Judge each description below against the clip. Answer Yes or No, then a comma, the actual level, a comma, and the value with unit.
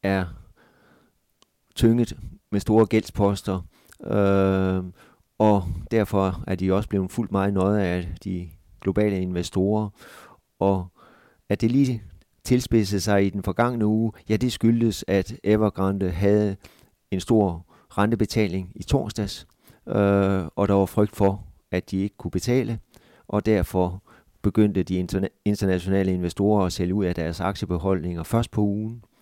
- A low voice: Yes, low, 100 Hz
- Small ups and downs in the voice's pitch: Yes, narrow, 2.3 semitones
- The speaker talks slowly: Yes, slow, 140 wpm